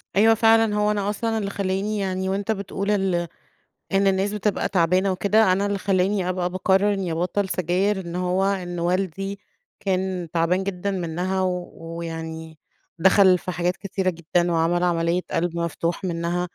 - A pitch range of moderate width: No, narrow, 2.2 semitones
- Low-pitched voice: No, medium, 185 Hz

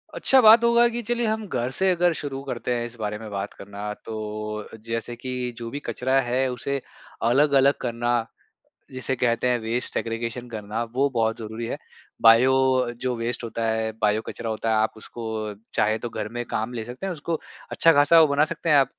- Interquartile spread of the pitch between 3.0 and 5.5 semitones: Yes, average, 3.7 semitones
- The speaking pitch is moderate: No, low, 120 Hz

